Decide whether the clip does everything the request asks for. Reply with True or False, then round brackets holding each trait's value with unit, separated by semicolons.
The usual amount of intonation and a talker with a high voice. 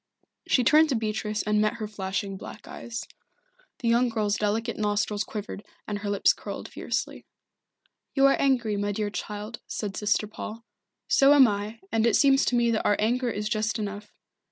False (2.2 semitones; 215 Hz)